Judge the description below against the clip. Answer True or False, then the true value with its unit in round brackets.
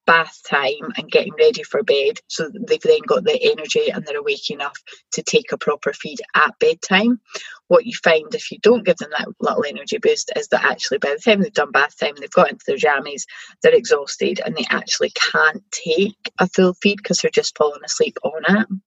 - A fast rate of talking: True (225 wpm)